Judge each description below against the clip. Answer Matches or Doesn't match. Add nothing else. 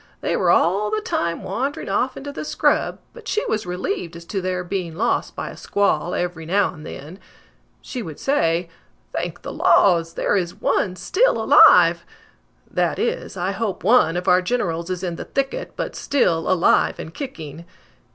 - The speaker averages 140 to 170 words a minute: Doesn't match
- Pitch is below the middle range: Doesn't match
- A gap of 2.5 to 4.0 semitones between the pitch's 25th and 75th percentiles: Doesn't match